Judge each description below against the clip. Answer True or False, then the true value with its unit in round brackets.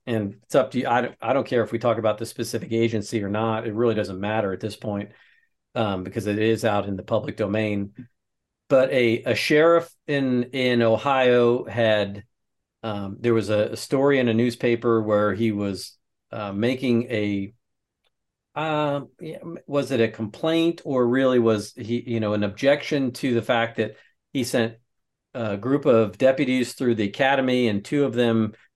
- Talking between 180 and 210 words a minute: True (185 wpm)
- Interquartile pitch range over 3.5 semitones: False (3.1 semitones)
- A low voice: True (115 Hz)